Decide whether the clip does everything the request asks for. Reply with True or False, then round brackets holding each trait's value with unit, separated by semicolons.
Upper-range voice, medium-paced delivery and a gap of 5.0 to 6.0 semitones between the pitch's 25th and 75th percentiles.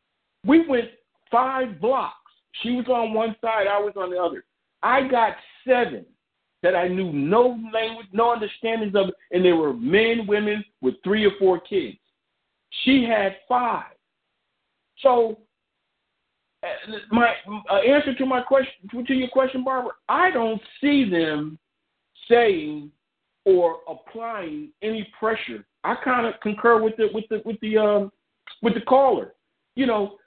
False (225 Hz; 150 wpm; 3.6 semitones)